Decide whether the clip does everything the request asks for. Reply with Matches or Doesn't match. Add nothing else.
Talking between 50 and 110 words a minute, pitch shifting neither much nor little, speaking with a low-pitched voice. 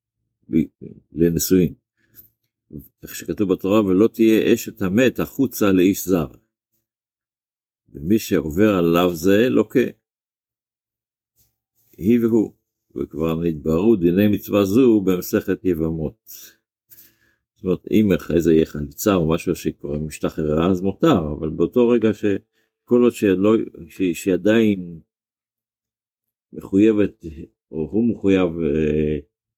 Matches